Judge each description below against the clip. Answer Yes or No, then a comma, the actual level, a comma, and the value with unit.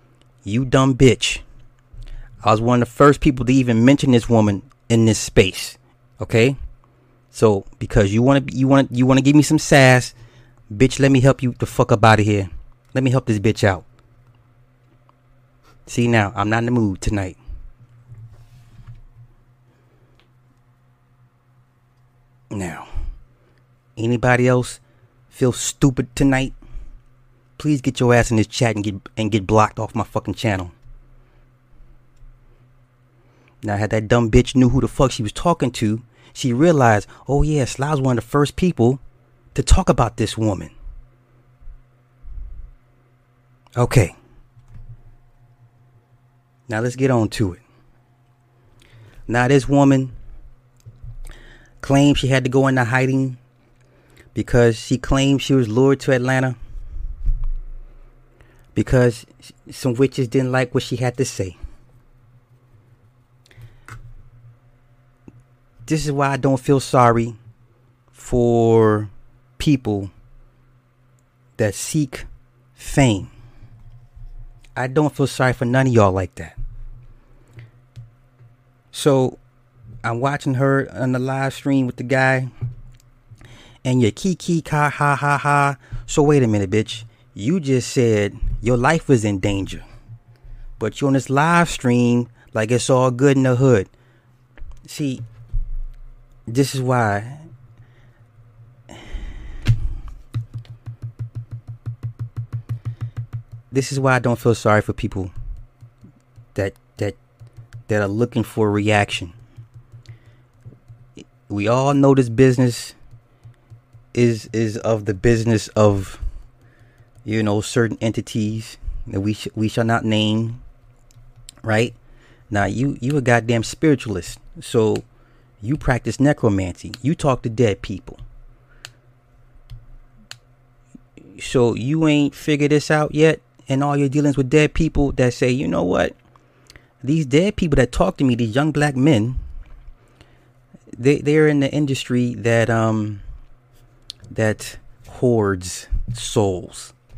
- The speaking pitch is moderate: No, low, 120 Hz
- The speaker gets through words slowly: Yes, slow, 125 wpm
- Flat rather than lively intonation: Yes, narrow, 1.8 semitones